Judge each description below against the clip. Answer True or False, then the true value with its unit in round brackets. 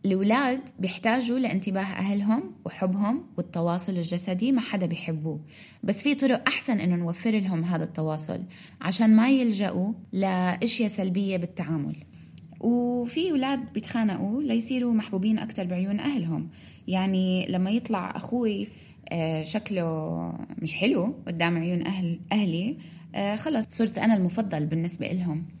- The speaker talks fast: False (115 wpm)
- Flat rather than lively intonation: False (4.6 semitones)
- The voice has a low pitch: False (195 Hz)